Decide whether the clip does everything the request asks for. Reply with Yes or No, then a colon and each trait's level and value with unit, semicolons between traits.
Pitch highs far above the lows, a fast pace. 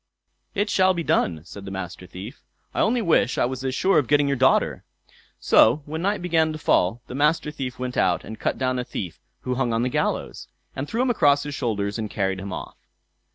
Yes: wide, 6.5 semitones; fast, 225 wpm